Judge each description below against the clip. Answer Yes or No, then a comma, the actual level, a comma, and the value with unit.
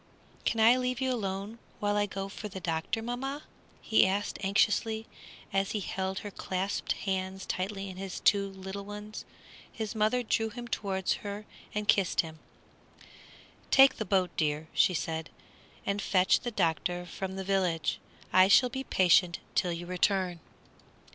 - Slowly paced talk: No, average, 160 wpm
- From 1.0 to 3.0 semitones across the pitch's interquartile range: Yes, narrow, 2.5 semitones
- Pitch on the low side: No, high, 195 Hz